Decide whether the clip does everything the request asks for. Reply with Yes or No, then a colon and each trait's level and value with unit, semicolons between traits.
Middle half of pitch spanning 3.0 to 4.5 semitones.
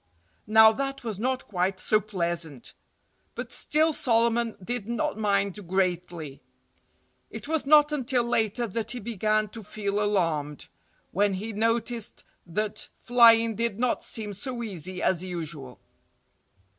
Yes: average, 4.1 semitones